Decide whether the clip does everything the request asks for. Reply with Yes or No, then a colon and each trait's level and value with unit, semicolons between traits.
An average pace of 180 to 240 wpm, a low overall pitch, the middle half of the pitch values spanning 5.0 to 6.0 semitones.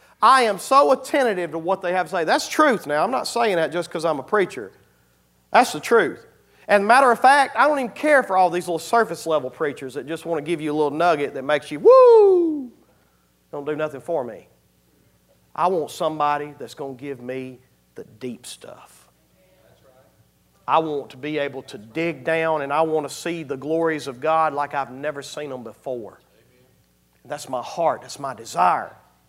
No: average, 200 wpm; medium, 155 Hz; wide, 5.4 semitones